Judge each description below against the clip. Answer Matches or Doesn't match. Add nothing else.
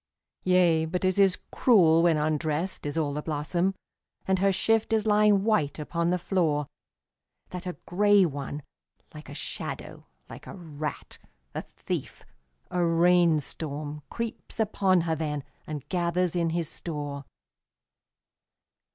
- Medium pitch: Matches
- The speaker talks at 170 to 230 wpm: Doesn't match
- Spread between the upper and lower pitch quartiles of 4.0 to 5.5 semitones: Doesn't match